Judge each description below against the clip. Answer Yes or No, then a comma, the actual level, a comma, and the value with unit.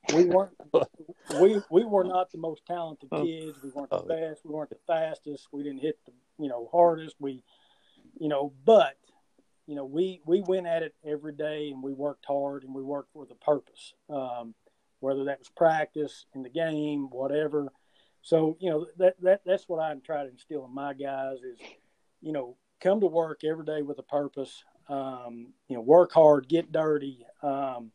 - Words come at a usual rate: Yes, average, 195 wpm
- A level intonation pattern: No, average, 3.1 semitones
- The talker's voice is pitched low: No, medium, 150 Hz